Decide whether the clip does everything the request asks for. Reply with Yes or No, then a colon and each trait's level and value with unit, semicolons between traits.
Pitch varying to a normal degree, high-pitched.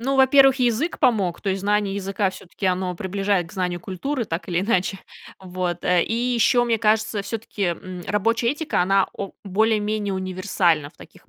Yes: average, 3.4 semitones; high, 200 Hz